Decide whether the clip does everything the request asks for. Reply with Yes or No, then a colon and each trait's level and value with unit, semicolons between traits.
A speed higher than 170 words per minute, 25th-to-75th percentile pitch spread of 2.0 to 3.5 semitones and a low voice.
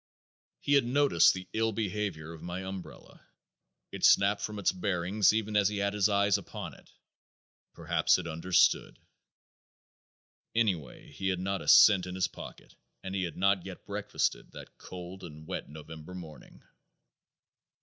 No: average, 155 wpm; average, 2.8 semitones; very low, 95 Hz